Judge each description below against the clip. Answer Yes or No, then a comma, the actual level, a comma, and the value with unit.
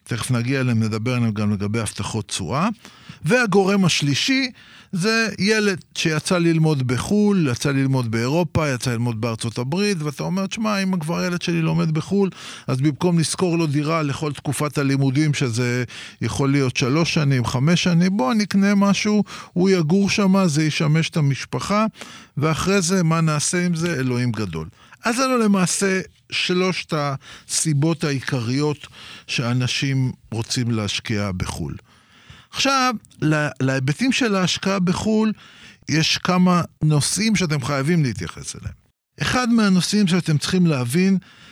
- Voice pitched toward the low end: No, medium, 155 Hz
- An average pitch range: No, wide, 6.5 semitones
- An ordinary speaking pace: Yes, average, 135 wpm